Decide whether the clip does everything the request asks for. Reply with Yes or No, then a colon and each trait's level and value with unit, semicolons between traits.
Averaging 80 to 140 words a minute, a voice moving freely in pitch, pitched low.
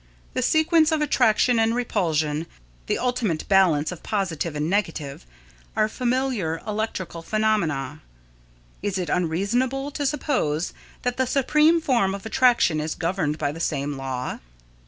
No: slow, 135 wpm; wide, 7.8 semitones; high, 200 Hz